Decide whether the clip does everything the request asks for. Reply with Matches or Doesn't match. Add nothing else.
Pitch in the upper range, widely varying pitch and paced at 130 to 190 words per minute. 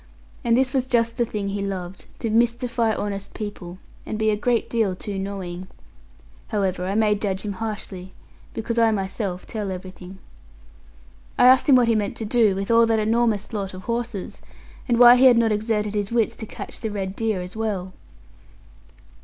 Doesn't match